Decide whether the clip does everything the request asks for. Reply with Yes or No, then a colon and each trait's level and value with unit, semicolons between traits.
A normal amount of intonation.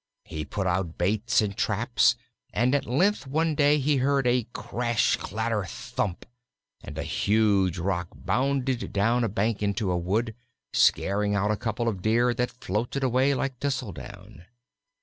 Yes: average, 4.3 semitones